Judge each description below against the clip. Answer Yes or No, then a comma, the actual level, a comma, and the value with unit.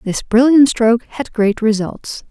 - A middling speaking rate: Yes, average, 155 wpm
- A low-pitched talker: No, high, 230 Hz